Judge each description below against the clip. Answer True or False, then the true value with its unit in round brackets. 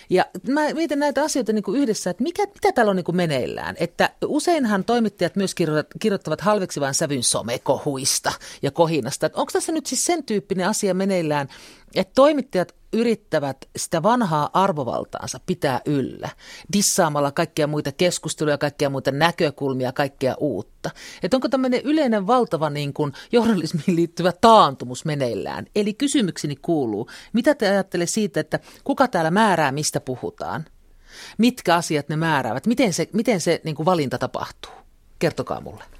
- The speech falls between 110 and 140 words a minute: False (150 wpm)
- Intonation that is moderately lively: False (7.2 semitones)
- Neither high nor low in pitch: True (180 Hz)